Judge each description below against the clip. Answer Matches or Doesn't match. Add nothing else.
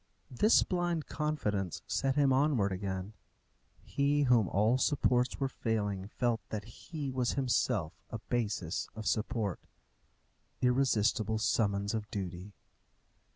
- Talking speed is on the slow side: Matches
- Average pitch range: Matches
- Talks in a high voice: Doesn't match